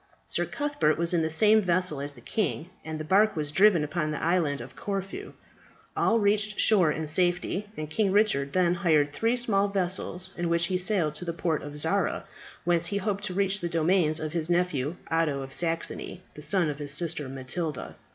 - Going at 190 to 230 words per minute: Yes, average, 200 wpm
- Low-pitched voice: No, medium, 170 Hz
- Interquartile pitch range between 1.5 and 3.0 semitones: No, average, 3.9 semitones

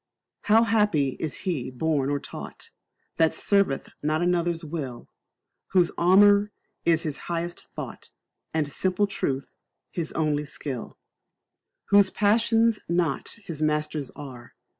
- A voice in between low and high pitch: Yes, medium, 165 Hz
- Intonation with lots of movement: No, average, 4.9 semitones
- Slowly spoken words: Yes, slow, 120 wpm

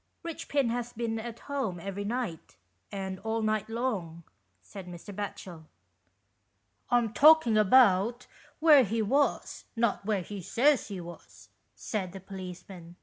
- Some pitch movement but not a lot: Yes, average, 4.5 semitones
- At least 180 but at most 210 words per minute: No, average, 145 wpm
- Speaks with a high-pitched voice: Yes, high, 210 Hz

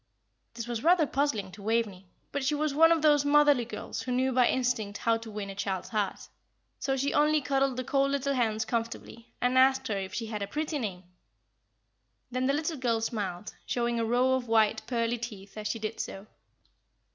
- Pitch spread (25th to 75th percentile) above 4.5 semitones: No, average, 4.0 semitones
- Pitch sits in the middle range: No, high, 240 Hz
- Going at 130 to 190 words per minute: No, fast, 205 wpm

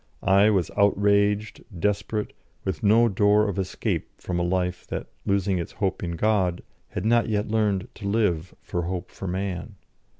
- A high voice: No, low, 100 Hz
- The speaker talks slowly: No, average, 165 wpm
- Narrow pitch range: Yes, narrow, 2.3 semitones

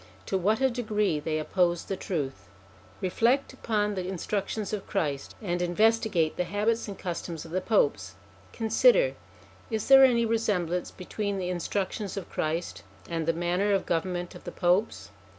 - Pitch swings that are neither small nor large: Yes, average, 4.0 semitones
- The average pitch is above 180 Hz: Yes, high, 190 Hz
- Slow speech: No, average, 165 wpm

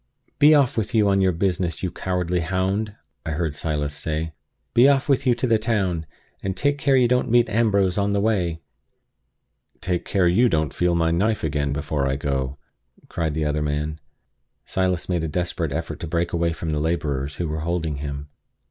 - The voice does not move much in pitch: No, average, 4.7 semitones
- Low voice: Yes, very low, 85 Hz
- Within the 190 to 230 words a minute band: Yes, average, 200 wpm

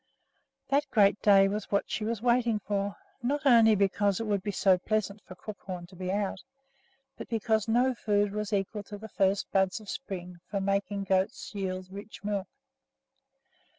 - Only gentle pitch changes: Yes, narrow, 2.0 semitones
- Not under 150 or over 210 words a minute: Yes, average, 175 wpm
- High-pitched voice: Yes, high, 205 Hz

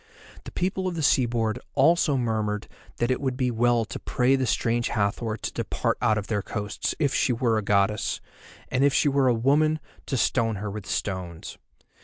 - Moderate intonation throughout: Yes, average, 4.0 semitones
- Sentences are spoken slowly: No, average, 195 wpm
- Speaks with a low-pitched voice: Yes, low, 120 Hz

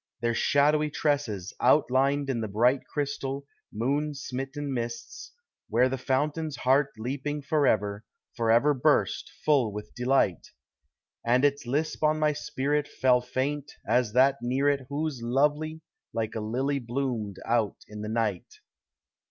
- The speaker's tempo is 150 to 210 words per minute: No, slow, 135 wpm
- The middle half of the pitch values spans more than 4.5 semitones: No, average, 3.6 semitones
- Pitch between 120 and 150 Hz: Yes, low, 135 Hz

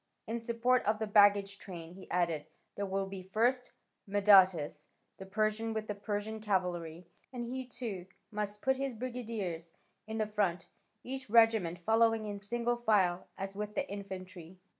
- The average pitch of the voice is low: No, high, 205 Hz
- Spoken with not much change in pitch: No, average, 3.2 semitones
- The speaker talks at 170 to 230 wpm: No, average, 160 wpm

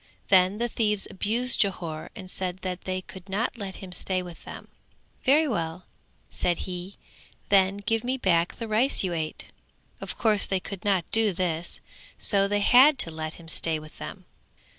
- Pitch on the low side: No, high, 190 Hz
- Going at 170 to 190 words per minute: Yes, average, 180 wpm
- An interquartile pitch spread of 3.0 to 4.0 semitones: Yes, average, 3.3 semitones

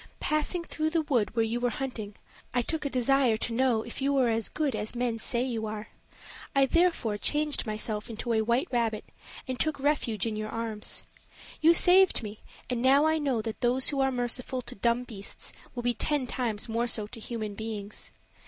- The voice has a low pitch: No, high, 240 Hz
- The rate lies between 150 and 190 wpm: No, average, 200 wpm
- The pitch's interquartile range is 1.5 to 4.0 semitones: Yes, average, 3.7 semitones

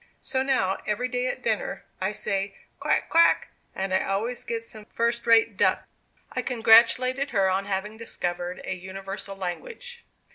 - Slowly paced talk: No, average, 155 wpm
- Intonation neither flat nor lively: Yes, average, 4.3 semitones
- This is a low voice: No, high, 215 Hz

